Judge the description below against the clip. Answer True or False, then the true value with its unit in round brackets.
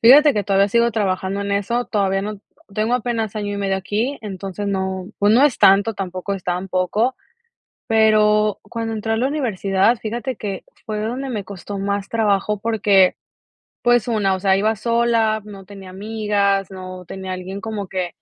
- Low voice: False (205 Hz)